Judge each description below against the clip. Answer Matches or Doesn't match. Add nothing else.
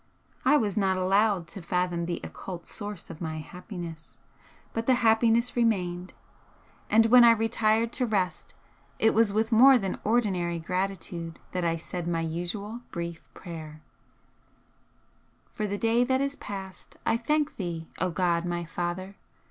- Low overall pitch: Doesn't match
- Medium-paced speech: Matches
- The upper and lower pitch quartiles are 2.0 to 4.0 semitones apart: Doesn't match